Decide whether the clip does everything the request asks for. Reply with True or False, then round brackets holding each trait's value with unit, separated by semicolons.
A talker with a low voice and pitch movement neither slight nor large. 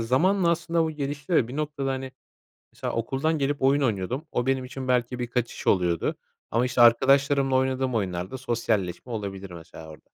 True (130 Hz; 3.5 semitones)